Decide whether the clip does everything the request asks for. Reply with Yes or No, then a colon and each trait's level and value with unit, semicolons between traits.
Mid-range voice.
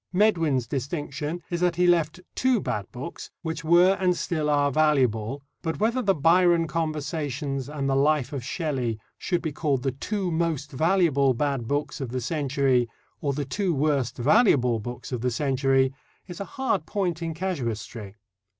Yes: medium, 150 Hz